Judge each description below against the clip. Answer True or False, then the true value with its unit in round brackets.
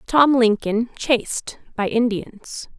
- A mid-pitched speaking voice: False (230 Hz)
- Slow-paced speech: True (110 wpm)